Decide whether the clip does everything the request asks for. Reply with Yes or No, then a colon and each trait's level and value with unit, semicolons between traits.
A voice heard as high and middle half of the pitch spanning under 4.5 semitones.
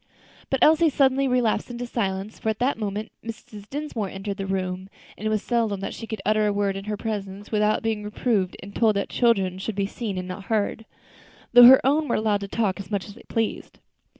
Yes: high, 215 Hz; average, 2.9 semitones